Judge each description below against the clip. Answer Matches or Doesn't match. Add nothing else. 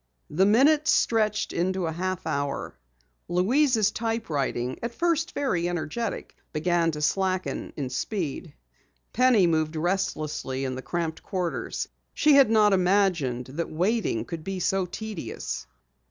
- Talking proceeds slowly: Matches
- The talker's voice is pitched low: Doesn't match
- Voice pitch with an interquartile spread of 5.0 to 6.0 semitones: Matches